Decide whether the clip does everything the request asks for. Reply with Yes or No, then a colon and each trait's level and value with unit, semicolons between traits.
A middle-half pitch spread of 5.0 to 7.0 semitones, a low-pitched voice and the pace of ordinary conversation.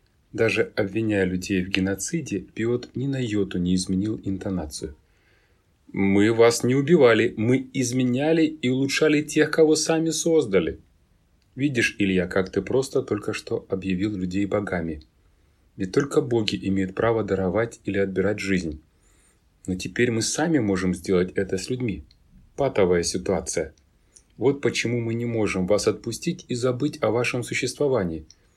Yes: average, 5.3 semitones; low, 100 Hz; average, 140 wpm